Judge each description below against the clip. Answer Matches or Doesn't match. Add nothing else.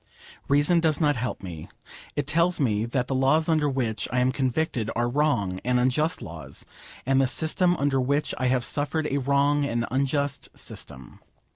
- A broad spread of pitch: Doesn't match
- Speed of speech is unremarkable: Matches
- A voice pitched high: Doesn't match